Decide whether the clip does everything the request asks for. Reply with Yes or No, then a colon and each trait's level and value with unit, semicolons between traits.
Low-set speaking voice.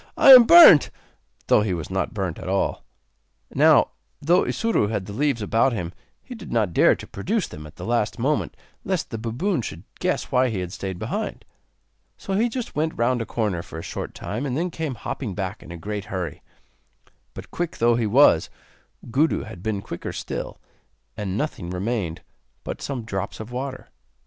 Yes: low, 115 Hz